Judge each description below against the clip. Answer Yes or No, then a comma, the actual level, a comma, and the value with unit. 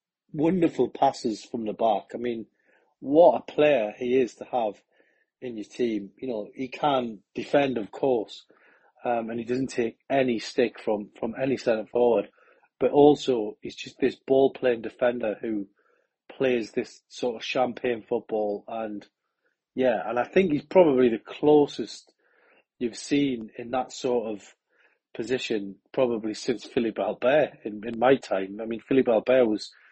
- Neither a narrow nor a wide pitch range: Yes, average, 3.1 semitones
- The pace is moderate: Yes, average, 160 wpm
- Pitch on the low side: Yes, low, 120 Hz